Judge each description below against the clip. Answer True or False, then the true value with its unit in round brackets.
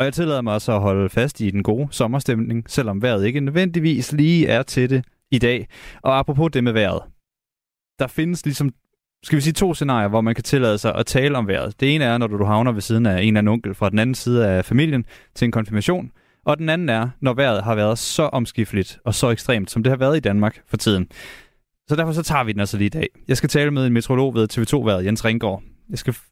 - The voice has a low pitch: True (120 Hz)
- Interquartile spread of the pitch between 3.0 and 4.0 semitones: False (4.5 semitones)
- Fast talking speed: True (250 wpm)